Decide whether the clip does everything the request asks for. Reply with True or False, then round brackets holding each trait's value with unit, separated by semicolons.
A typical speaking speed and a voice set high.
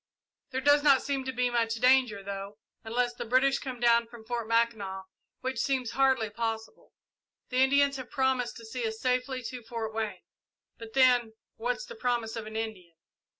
True (180 wpm; 240 Hz)